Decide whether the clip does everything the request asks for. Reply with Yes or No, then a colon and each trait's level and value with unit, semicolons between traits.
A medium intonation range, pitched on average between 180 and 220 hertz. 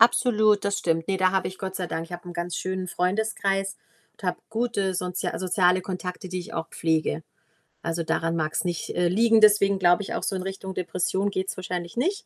No: narrow, 2.1 semitones; medium, 185 Hz